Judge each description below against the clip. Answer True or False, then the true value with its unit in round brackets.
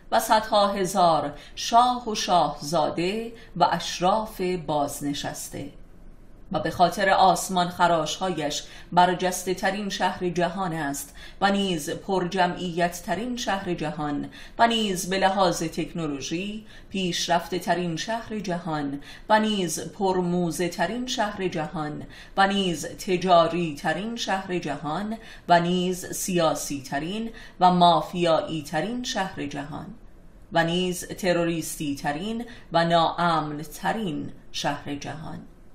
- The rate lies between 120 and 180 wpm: False (110 wpm)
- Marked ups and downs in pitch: False (3.4 semitones)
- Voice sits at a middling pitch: True (175 Hz)